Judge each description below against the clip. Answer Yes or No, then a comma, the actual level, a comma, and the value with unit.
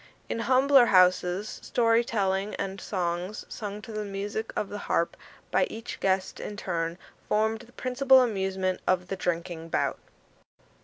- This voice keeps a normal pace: Yes, average, 150 wpm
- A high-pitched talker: Yes, high, 200 Hz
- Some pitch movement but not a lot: Yes, average, 3.6 semitones